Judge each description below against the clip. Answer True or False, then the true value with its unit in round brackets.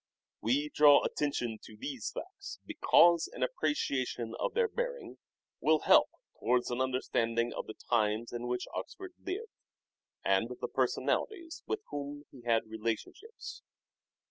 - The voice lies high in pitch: False (140 Hz)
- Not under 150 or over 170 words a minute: False (135 wpm)